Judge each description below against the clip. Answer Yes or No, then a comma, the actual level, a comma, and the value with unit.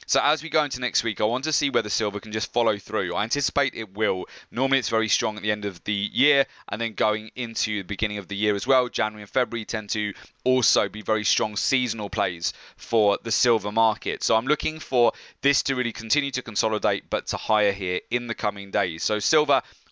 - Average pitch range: Yes, average, 3.5 semitones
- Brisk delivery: Yes, fast, 230 wpm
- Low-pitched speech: Yes, low, 110 Hz